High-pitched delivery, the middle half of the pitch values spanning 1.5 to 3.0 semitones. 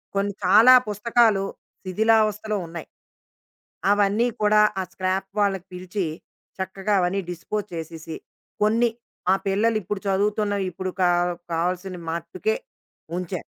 Yes: high, 195 Hz; narrow, 2.6 semitones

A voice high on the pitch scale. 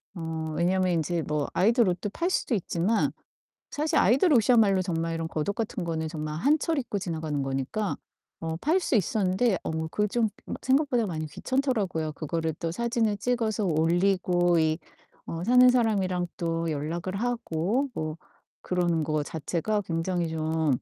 No: medium, 180 Hz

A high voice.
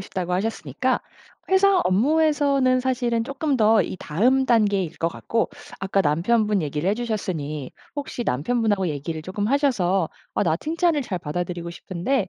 Yes: high, 210 Hz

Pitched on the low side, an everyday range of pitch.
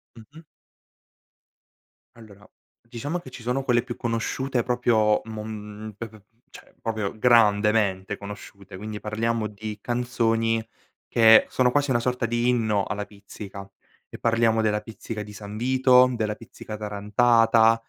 No: low, 110 Hz; narrow, 2.2 semitones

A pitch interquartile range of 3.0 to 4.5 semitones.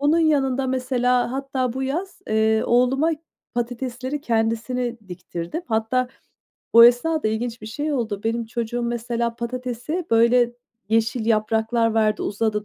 No: narrow, 2.4 semitones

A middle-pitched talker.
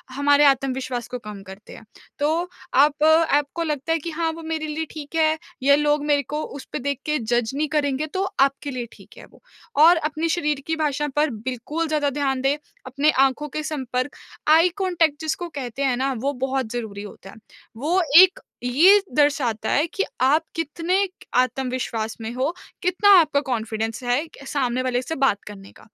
No: very high, 285 Hz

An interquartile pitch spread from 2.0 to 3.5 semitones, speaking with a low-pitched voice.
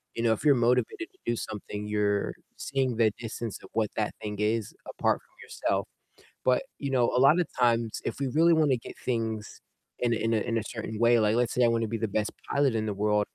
Yes: narrow, 2.6 semitones; low, 115 Hz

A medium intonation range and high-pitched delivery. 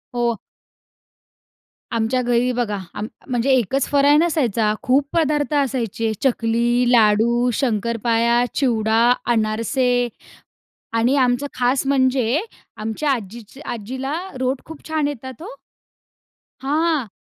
Yes: average, 3.1 semitones; high, 245 Hz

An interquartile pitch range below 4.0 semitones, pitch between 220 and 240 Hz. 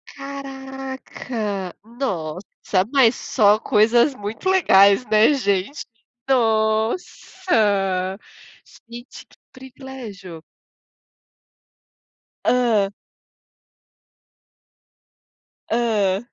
No: average, 4.9 semitones; high, 225 Hz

